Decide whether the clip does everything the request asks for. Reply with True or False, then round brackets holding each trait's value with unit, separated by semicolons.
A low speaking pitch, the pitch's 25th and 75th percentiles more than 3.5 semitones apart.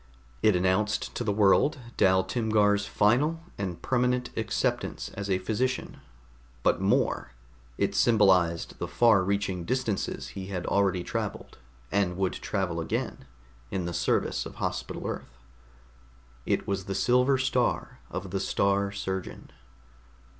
False (100 Hz; 3.2 semitones)